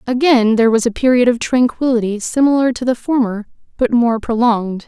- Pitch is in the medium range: No, high, 240 Hz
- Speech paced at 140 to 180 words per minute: Yes, average, 170 wpm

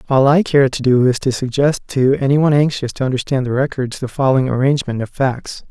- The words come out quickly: Yes, fast, 220 wpm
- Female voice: No, male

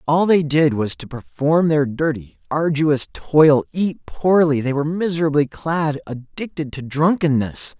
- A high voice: No, medium, 150 Hz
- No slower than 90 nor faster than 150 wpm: Yes, average, 145 wpm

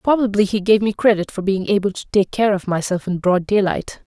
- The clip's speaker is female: Yes, female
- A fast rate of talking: Yes, fast, 230 wpm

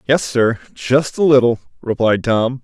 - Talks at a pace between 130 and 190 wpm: Yes, slow, 135 wpm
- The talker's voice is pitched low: Yes, low, 120 Hz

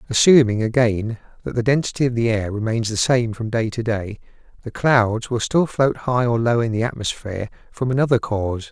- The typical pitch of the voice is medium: No, low, 115 Hz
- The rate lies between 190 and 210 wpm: Yes, average, 200 wpm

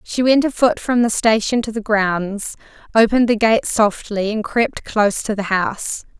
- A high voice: Yes, high, 220 Hz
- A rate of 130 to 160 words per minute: No, average, 185 wpm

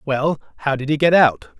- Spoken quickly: Yes, fast, 225 wpm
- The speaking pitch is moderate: Yes, medium, 145 Hz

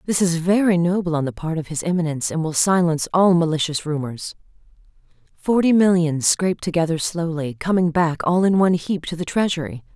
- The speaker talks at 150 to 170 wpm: No, average, 180 wpm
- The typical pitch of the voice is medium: Yes, medium, 165 Hz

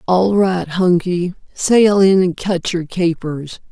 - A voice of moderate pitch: Yes, medium, 180 Hz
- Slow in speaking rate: Yes, slow, 130 wpm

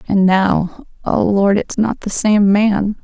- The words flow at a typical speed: Yes, average, 180 wpm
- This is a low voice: No, high, 205 Hz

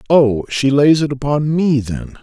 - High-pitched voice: No, medium, 140 Hz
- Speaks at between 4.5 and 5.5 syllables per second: No, 4.1 syllables/s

